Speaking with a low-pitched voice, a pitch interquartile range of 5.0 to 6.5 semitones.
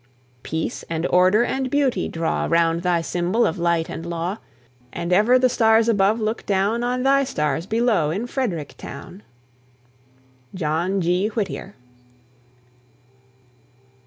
No: high, 190 Hz; wide, 5.4 semitones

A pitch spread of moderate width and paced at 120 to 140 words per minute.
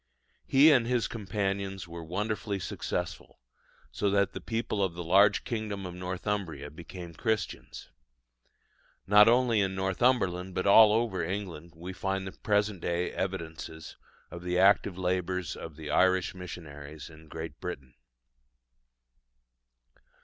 Yes: average, 3.1 semitones; slow, 135 wpm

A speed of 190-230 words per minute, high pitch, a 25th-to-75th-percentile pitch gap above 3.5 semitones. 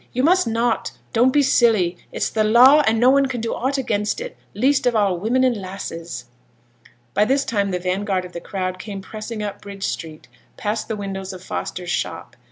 Yes: average, 200 wpm; high, 215 Hz; average, 4.4 semitones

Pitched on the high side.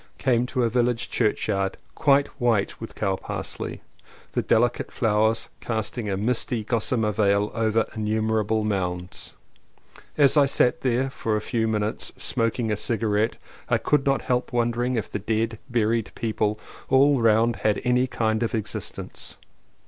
No: low, 115 Hz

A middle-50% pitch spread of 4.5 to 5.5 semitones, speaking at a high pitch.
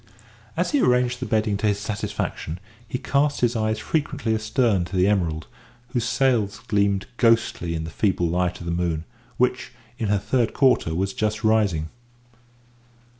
No: average, 4.9 semitones; low, 105 Hz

